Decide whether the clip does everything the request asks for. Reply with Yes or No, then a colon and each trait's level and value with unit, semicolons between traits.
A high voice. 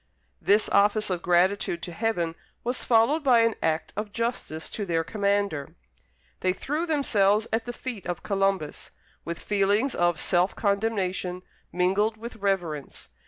Yes: high, 200 Hz